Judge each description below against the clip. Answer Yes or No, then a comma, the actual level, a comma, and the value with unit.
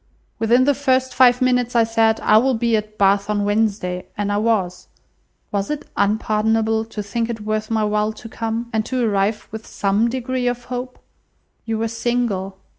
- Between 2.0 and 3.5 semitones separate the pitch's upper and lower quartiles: Yes, narrow, 2.4 semitones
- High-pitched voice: Yes, high, 225 Hz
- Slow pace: No, average, 185 wpm